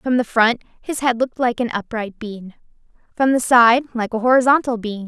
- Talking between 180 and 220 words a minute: Yes, average, 200 wpm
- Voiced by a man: No, female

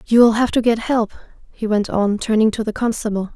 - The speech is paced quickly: Yes, fast, 215 wpm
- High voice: Yes, high, 220 Hz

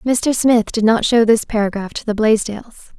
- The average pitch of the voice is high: Yes, high, 225 Hz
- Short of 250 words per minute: Yes, average, 200 wpm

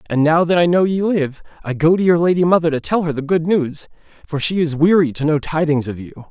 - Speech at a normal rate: No, fast, 265 wpm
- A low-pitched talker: No, medium, 160 Hz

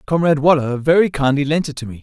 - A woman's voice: No, male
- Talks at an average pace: No, fast, 235 wpm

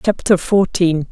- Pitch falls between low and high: Yes, medium, 180 Hz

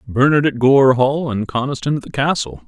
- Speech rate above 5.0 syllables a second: Yes, 5.2 syllables/s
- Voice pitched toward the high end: No, low, 135 Hz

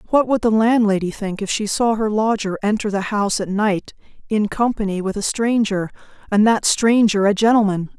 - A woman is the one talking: Yes, female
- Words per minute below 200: Yes, average, 190 wpm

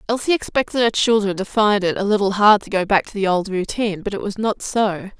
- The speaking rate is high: Yes, fast, 255 wpm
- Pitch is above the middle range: Yes, high, 205 Hz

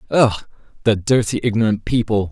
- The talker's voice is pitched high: No, low, 110 Hz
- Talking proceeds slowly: Yes, slow, 130 wpm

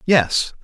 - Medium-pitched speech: Yes, medium, 155 Hz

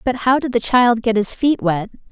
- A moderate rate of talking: No, fast, 255 wpm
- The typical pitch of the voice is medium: No, high, 235 Hz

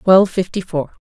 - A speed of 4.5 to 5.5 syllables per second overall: Yes, 5.4 syllables/s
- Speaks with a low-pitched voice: No, medium, 185 Hz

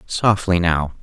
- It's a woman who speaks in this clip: No, male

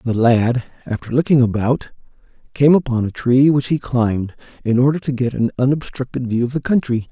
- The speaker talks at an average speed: Yes, average, 185 wpm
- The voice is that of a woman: No, male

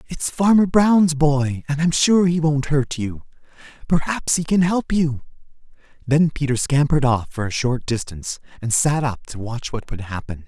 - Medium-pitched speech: Yes, medium, 145 Hz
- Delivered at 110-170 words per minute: No, average, 185 wpm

